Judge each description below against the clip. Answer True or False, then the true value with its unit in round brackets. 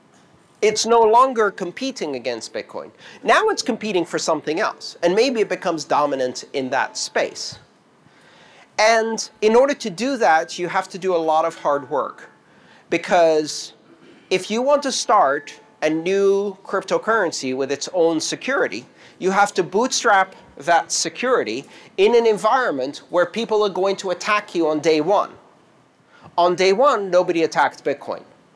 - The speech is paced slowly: False (155 wpm)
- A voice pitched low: False (190 Hz)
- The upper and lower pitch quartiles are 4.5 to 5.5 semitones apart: True (5.2 semitones)